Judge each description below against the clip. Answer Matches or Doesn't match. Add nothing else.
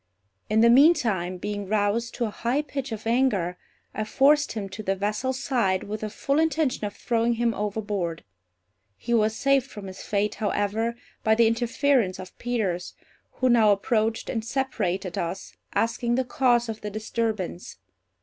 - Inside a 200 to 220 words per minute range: Doesn't match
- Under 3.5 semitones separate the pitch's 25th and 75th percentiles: Matches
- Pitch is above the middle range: Matches